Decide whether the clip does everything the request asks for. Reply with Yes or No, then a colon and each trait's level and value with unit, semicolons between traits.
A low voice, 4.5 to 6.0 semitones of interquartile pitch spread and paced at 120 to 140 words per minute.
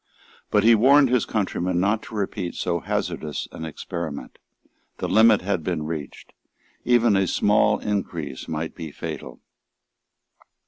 Yes: very low, 95 Hz; average, 5.0 semitones; slow, 135 wpm